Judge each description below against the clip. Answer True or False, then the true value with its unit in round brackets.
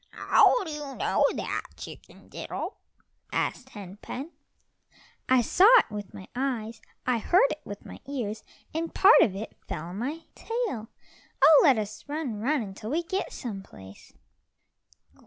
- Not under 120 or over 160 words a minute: True (155 wpm)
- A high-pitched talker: True (250 Hz)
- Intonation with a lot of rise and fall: True (6.5 semitones)